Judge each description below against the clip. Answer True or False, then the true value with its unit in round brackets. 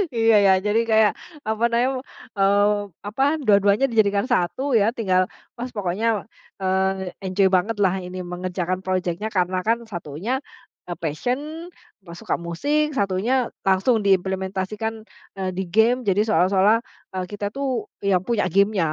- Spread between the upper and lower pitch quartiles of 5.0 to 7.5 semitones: False (2.9 semitones)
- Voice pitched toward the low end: False (195 Hz)